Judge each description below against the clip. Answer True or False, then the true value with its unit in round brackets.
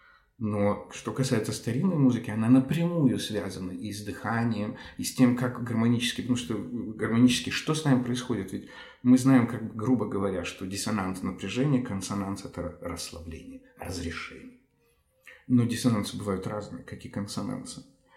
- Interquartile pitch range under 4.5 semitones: True (3.8 semitones)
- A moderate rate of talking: True (140 wpm)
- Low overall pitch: True (115 Hz)